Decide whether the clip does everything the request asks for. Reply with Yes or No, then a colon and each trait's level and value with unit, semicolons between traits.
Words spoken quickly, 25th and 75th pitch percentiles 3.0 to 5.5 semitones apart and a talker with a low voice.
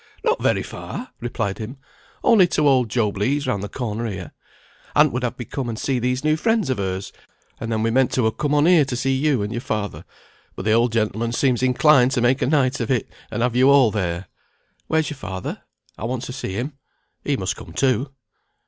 Yes: fast, 225 wpm; average, 3.9 semitones; low, 125 Hz